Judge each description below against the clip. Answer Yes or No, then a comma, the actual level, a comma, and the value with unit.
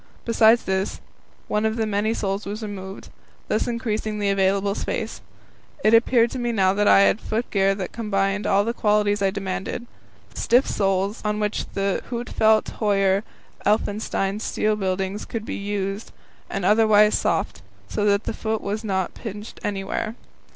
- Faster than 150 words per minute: Yes, average, 160 wpm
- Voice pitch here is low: No, high, 205 Hz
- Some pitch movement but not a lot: No, narrow, 1.9 semitones